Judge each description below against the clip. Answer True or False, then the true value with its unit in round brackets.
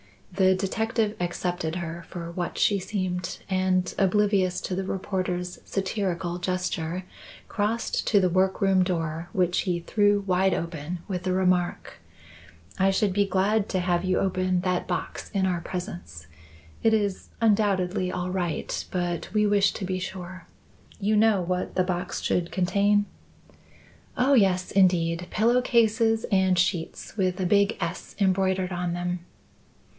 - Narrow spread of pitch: True (2.0 semitones)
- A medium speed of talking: True (150 wpm)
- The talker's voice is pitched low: False (185 Hz)